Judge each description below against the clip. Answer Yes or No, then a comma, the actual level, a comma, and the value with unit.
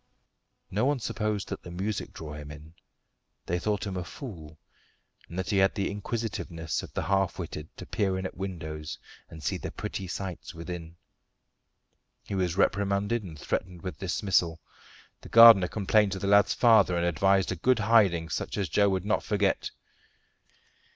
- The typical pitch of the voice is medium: No, very low, 95 Hz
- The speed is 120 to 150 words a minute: No, average, 170 wpm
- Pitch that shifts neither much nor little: Yes, average, 3.1 semitones